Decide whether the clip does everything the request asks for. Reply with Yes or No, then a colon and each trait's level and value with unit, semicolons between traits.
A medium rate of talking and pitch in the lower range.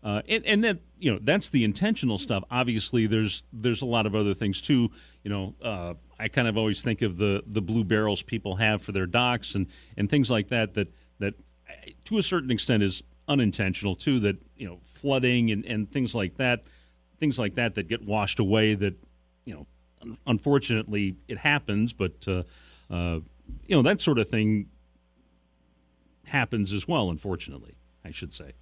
Yes: average, 190 wpm; low, 105 Hz